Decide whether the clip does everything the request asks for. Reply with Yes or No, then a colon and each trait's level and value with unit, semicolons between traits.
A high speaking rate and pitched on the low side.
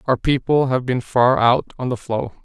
Yes: fast, 220 wpm; low, 125 Hz